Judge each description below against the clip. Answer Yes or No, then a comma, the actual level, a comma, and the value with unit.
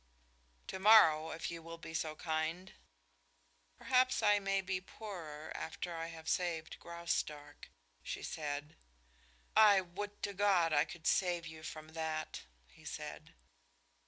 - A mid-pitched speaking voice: Yes, medium, 165 Hz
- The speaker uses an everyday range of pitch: Yes, average, 3.3 semitones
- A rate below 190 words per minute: Yes, slow, 135 wpm